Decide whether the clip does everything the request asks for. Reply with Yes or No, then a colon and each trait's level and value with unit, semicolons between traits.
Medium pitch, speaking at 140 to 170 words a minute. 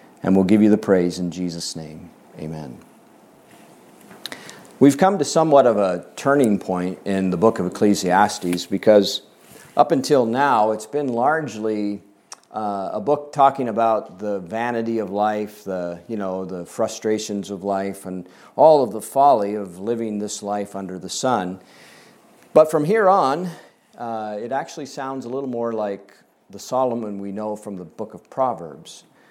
No: low, 105 Hz; average, 160 wpm